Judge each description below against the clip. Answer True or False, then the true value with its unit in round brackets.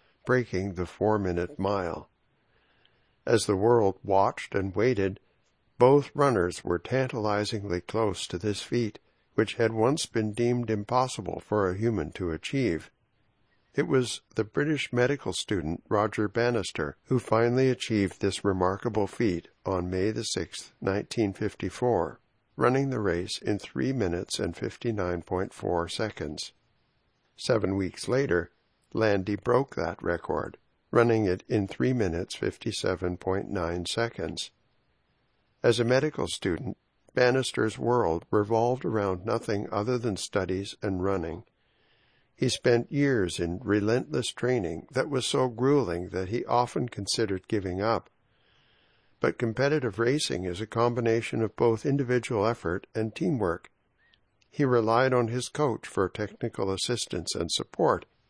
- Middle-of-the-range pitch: False (110 Hz)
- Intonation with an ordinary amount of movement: True (4.2 semitones)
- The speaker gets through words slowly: True (125 wpm)